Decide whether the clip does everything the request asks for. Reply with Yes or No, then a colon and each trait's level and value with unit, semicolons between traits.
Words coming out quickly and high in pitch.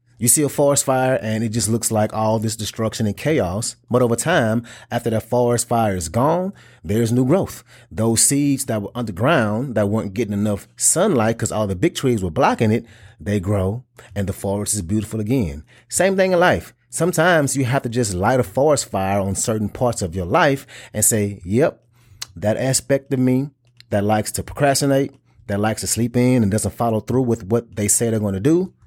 No: fast, 210 wpm; low, 115 Hz